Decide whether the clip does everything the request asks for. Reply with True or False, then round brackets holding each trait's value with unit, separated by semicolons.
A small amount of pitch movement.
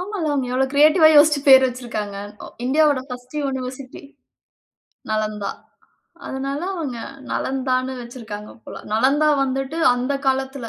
True (2.3 semitones)